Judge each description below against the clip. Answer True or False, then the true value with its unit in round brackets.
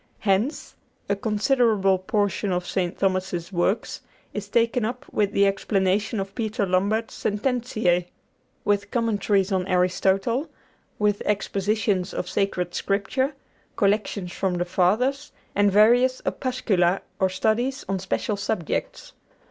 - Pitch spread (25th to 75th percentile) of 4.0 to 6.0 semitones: False (2.8 semitones)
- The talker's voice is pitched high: True (200 Hz)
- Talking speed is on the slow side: True (120 wpm)